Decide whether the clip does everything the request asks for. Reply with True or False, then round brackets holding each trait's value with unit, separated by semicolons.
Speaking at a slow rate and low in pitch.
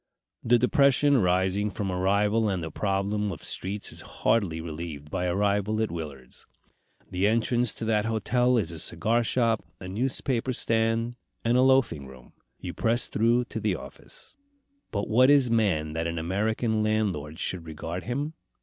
False (160 wpm; 105 Hz)